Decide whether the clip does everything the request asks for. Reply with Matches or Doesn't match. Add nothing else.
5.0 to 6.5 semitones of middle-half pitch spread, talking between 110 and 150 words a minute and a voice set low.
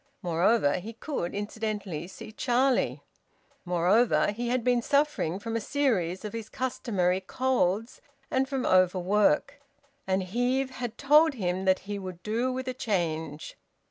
Doesn't match